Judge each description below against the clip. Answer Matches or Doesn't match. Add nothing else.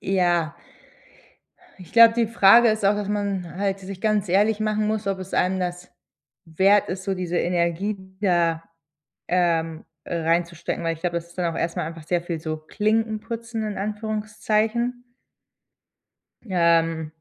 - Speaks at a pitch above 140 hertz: Matches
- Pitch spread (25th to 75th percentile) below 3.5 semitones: Doesn't match